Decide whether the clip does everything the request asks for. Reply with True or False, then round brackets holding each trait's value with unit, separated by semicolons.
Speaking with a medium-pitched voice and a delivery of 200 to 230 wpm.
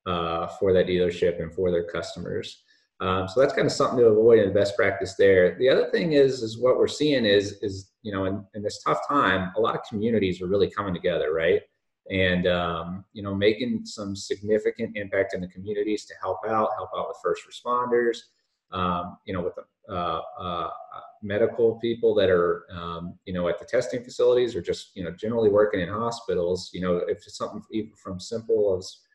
False (115 Hz; 205 wpm)